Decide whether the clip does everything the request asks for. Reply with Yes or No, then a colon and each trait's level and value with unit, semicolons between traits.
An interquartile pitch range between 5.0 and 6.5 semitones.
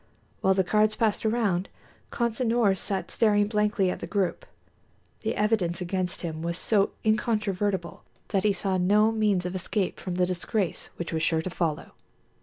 No: average, 2.9 semitones